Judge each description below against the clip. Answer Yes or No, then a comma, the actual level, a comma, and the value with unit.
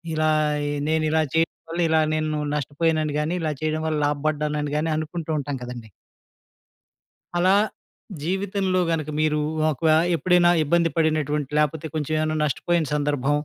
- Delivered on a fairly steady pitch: Yes, narrow, 1.7 semitones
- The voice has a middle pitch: Yes, medium, 155 Hz